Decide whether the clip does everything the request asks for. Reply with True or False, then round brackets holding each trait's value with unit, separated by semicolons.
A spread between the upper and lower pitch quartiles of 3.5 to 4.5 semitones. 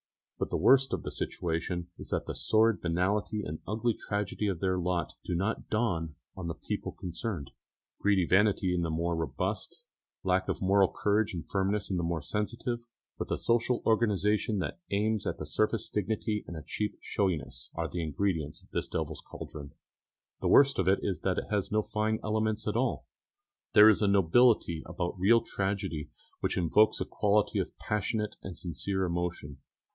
True (3.8 semitones)